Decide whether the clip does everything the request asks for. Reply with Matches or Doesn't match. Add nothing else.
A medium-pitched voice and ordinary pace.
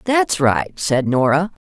Matches